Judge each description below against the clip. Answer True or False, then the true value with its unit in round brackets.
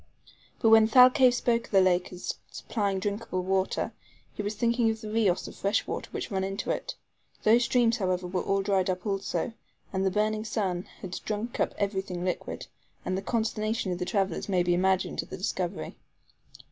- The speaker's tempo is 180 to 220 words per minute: True (190 wpm)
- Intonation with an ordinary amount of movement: True (3.0 semitones)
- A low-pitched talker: False (200 Hz)